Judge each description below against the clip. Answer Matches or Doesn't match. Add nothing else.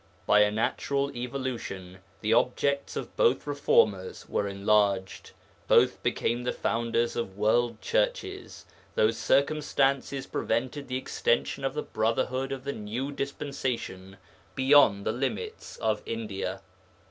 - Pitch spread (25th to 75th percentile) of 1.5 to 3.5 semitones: Doesn't match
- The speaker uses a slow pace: Matches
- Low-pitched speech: Matches